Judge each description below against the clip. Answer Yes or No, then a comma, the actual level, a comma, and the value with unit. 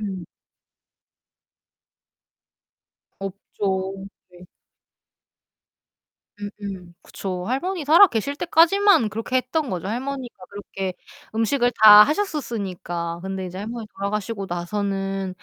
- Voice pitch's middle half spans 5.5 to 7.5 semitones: No, average, 5.1 semitones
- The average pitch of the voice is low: No, high, 205 Hz